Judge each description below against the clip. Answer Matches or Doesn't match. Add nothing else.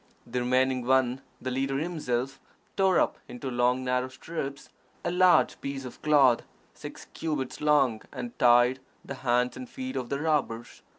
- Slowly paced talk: Doesn't match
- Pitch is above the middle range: Doesn't match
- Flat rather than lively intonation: Doesn't match